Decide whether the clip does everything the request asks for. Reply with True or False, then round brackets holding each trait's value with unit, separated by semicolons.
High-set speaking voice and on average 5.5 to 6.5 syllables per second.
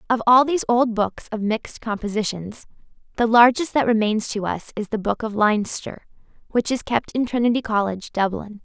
False (225 Hz; 5.3 syllables/s)